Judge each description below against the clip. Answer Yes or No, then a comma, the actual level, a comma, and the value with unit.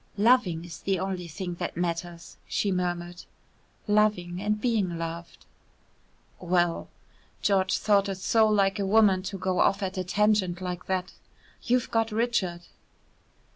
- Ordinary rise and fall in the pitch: Yes, average, 3.0 semitones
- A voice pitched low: No, high, 190 Hz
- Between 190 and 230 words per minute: No, average, 140 wpm